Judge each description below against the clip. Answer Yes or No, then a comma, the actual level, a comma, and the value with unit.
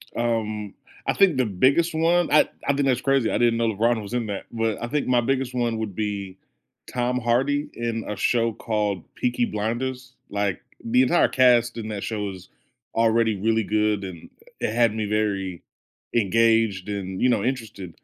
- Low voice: Yes, low, 115 Hz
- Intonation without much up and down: No, average, 3.1 semitones